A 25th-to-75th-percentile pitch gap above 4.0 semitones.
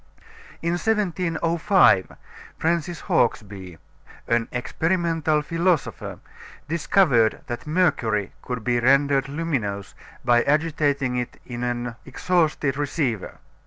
Yes: wide, 5.6 semitones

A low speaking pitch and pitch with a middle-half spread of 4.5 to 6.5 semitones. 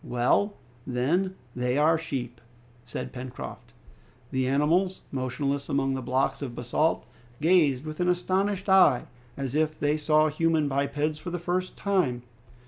No: medium, 150 Hz; average, 5.0 semitones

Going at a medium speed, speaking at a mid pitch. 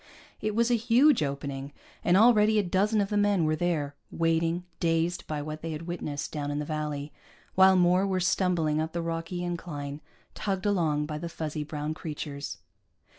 Yes: average, 180 wpm; medium, 165 Hz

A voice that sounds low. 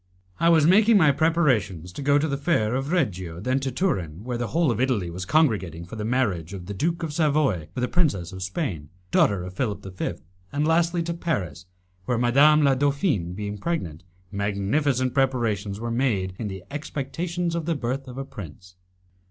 Yes: low, 125 Hz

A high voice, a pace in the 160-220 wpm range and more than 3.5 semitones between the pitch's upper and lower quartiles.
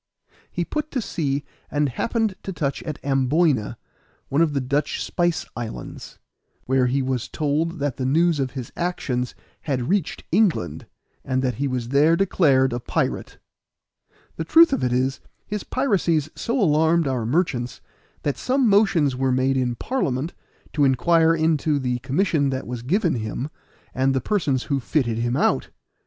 No: medium, 140 Hz; average, 165 wpm; average, 4.7 semitones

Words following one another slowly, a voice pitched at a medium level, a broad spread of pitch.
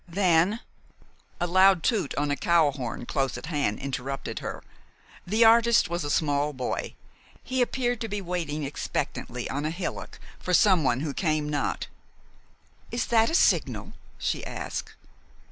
No: average, 150 wpm; medium, 165 Hz; wide, 5.9 semitones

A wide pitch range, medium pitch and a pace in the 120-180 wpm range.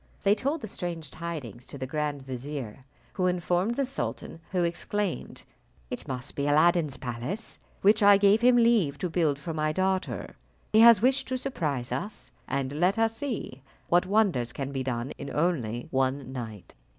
Yes: wide, 7.1 semitones; medium, 165 Hz; average, 175 wpm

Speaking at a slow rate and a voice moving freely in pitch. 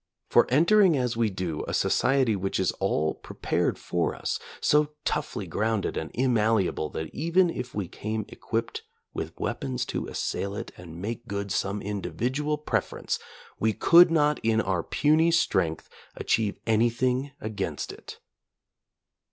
No: average, 145 wpm; wide, 6.4 semitones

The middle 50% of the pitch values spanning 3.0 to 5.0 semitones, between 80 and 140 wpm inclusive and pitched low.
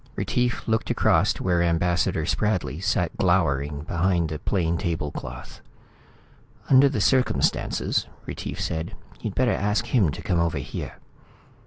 Yes: average, 4.6 semitones; slow, 135 wpm; very low, 85 Hz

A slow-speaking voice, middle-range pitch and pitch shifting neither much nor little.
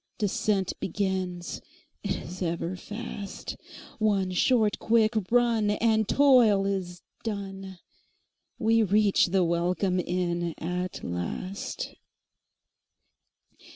No: slow, 85 wpm; high, 195 Hz; average, 3.1 semitones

